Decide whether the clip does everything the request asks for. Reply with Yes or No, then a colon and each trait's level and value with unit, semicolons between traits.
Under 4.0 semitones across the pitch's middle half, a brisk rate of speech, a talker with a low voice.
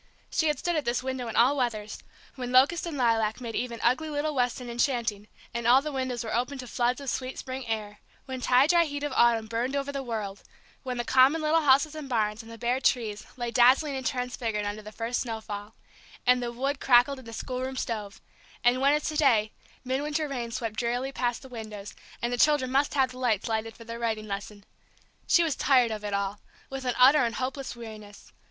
No: average, 3.0 semitones; fast, 220 wpm; high, 245 Hz